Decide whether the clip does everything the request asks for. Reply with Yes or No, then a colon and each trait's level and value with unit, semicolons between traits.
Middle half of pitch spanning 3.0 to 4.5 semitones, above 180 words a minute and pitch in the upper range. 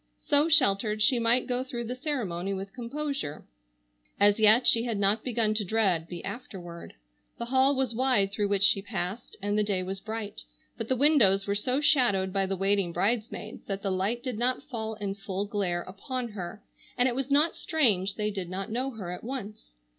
Yes: average, 4.2 semitones; average, 200 wpm; high, 215 Hz